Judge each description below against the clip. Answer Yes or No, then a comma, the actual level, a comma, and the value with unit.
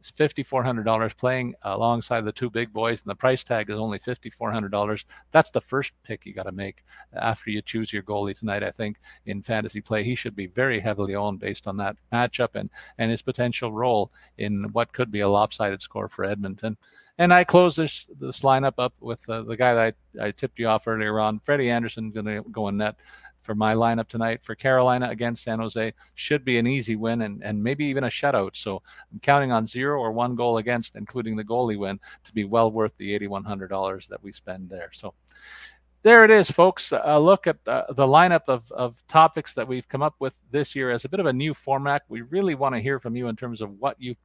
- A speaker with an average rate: No, fast, 230 wpm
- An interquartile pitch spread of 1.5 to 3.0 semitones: No, average, 3.4 semitones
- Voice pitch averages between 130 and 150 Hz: No, low, 115 Hz